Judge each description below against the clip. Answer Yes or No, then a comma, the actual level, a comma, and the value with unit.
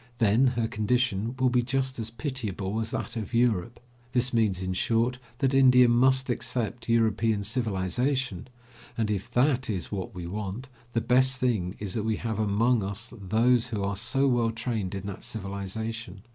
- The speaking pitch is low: Yes, low, 115 Hz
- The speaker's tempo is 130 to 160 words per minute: No, average, 175 wpm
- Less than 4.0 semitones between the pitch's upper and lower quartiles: Yes, average, 3.6 semitones